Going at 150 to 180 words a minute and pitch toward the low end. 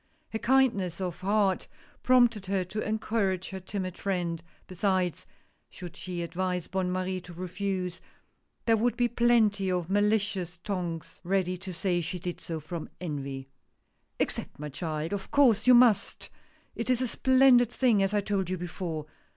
No: average, 165 wpm; high, 190 Hz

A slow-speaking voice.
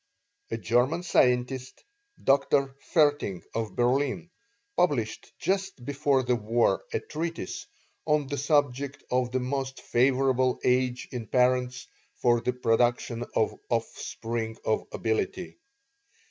Yes: slow, 115 wpm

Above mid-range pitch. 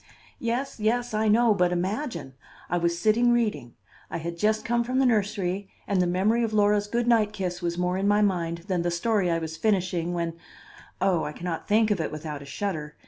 Yes: high, 195 Hz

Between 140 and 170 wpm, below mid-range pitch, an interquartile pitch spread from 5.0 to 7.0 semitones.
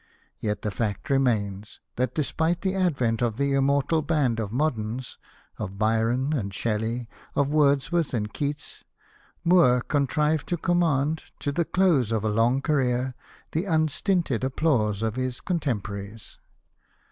Yes: average, 145 wpm; low, 130 Hz; wide, 5.5 semitones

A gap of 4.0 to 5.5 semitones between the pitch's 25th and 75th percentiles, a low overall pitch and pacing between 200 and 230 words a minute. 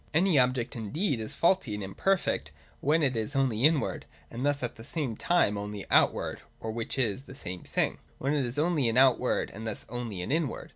Yes: average, 4.8 semitones; low, 125 Hz; fast, 205 wpm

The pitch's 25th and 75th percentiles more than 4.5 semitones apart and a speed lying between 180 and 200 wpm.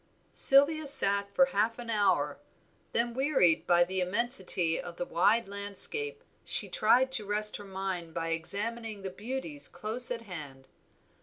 No: average, 5.3 semitones; average, 150 wpm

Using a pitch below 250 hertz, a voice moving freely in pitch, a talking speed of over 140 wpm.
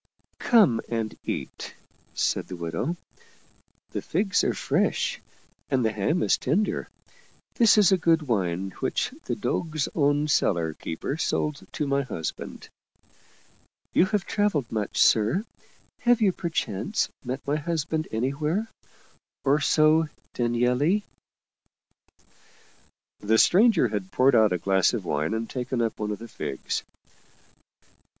No: low, 135 Hz; wide, 7.2 semitones; slow, 135 wpm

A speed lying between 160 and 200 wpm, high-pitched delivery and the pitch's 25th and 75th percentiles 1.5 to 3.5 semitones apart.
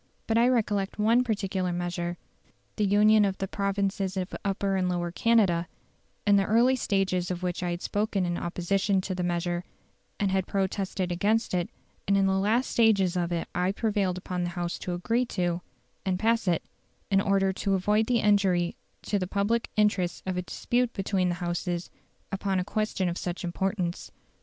Yes: average, 185 wpm; high, 195 Hz; narrow, 2.6 semitones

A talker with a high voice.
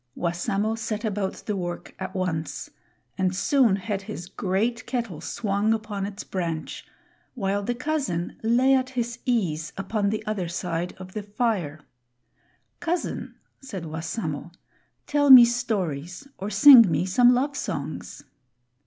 Yes: high, 205 Hz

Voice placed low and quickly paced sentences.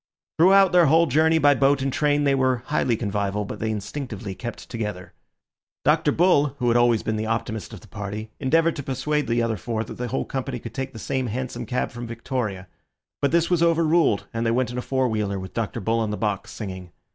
Yes: low, 120 Hz; fast, 225 wpm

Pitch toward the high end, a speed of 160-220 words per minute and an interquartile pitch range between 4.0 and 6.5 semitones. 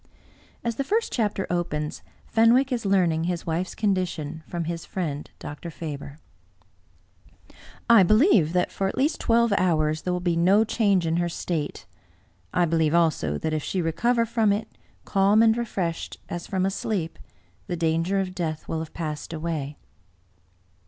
No: medium, 175 Hz; average, 170 wpm; average, 4.4 semitones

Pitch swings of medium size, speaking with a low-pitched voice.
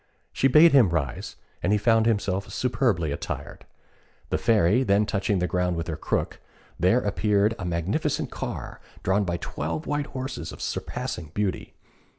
Yes: average, 5.0 semitones; low, 100 Hz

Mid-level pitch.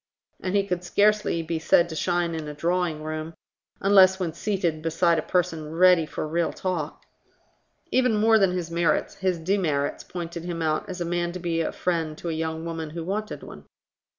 Yes: medium, 170 Hz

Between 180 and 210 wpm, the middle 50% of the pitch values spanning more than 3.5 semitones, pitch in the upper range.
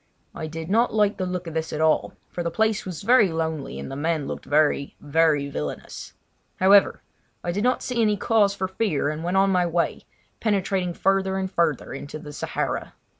No: average, 200 wpm; average, 4.0 semitones; medium, 175 Hz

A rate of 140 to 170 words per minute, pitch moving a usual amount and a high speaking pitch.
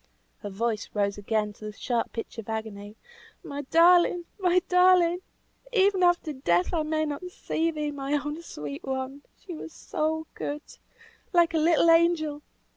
No: average, 160 wpm; wide, 7.0 semitones; very high, 300 Hz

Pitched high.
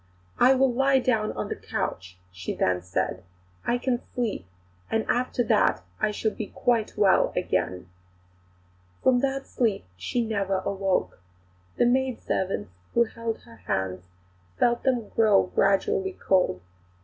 Yes: high, 215 Hz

